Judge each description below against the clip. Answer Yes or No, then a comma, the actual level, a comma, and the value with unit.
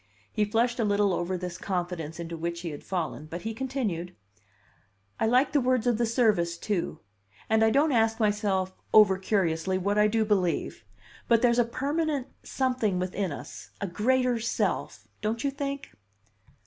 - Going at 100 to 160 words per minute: No, average, 170 wpm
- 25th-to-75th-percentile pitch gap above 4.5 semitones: Yes, average, 5.1 semitones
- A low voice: No, high, 210 Hz